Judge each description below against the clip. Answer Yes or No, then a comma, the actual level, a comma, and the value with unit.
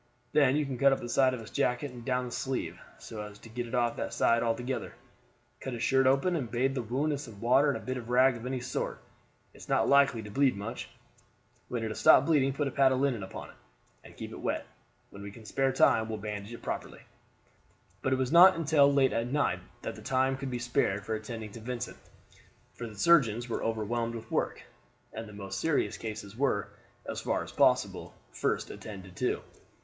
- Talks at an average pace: No, fast, 225 wpm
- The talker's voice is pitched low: Yes, low, 125 Hz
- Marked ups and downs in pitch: No, average, 3.2 semitones